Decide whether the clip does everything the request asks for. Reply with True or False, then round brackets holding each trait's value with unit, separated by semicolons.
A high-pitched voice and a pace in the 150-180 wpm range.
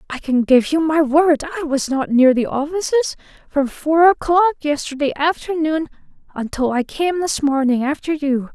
True (300 Hz; 170 wpm)